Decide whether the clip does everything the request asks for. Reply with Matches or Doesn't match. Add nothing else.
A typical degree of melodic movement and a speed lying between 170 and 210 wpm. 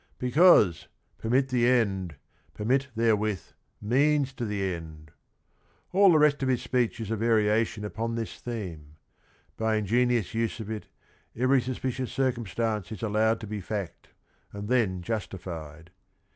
Doesn't match